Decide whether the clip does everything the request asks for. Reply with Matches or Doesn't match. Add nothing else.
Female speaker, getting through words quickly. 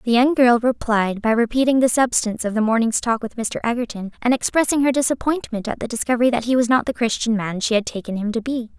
Matches